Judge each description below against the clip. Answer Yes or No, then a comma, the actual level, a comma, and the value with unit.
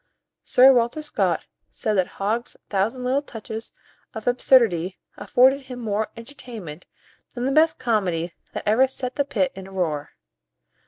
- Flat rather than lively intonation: No, average, 5.0 semitones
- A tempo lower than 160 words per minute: Yes, average, 150 wpm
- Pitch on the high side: Yes, high, 230 Hz